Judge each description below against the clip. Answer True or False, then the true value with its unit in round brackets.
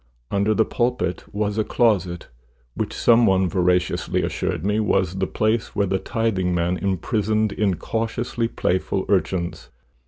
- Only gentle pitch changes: False (3.0 semitones)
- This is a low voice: True (100 Hz)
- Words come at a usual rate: False (130 wpm)